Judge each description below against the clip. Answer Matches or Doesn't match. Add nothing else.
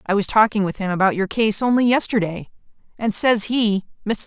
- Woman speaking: Matches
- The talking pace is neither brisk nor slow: Matches